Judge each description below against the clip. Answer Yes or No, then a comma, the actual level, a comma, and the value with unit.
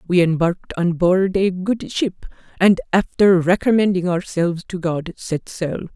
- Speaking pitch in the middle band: Yes, medium, 180 Hz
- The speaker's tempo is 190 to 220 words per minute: No, average, 150 wpm